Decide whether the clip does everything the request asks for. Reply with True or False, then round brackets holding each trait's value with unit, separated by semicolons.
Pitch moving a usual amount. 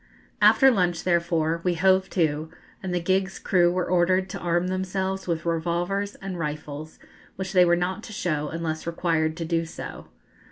False (2.2 semitones)